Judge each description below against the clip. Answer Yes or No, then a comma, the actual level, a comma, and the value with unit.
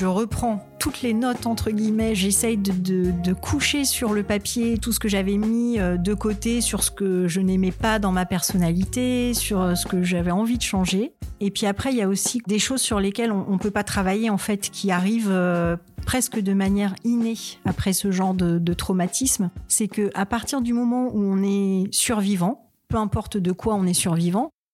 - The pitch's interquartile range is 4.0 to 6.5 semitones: No, average, 3.3 semitones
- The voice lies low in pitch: No, high, 205 Hz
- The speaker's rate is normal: Yes, average, 210 wpm